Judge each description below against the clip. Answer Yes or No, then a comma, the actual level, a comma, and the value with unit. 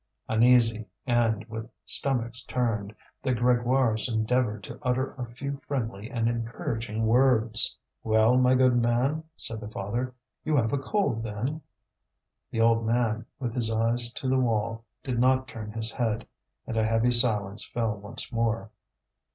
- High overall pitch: No, low, 115 Hz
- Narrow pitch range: Yes, narrow, 2.1 semitones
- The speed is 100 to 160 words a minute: Yes, average, 150 wpm